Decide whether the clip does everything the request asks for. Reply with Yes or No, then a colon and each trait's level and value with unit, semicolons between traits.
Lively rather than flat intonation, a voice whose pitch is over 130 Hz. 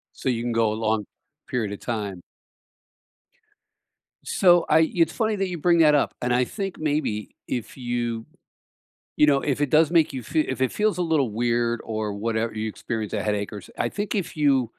No: wide, 6.1 semitones; low, 125 Hz